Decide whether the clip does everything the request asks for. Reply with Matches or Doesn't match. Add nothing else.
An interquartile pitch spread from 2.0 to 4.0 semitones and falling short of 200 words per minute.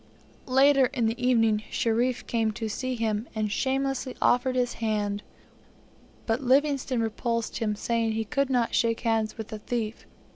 Matches